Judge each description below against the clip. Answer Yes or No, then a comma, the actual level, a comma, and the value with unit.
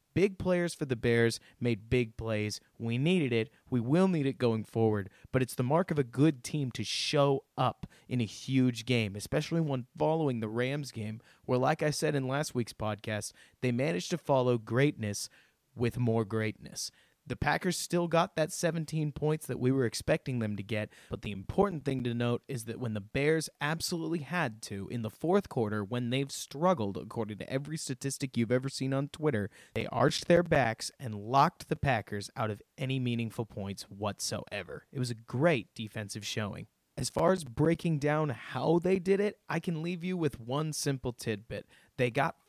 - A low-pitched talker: Yes, low, 130 Hz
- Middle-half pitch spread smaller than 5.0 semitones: No, wide, 5.5 semitones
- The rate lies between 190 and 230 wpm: Yes, average, 195 wpm